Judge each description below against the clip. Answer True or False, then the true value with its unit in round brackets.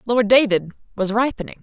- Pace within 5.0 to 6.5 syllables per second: True (5.5 syllables/s)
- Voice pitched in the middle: False (220 Hz)